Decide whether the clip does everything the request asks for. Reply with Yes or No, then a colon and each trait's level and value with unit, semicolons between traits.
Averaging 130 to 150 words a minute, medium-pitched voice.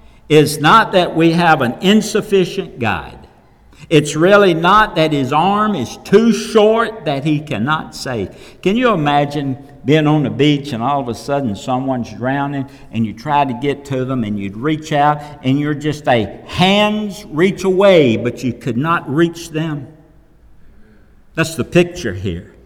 No: average, 165 wpm; medium, 150 Hz